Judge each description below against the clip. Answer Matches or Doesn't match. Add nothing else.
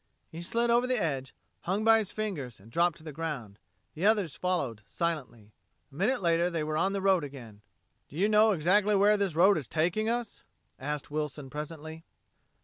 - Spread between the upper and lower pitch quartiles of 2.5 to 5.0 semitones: Doesn't match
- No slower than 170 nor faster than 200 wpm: Matches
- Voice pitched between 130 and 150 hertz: Doesn't match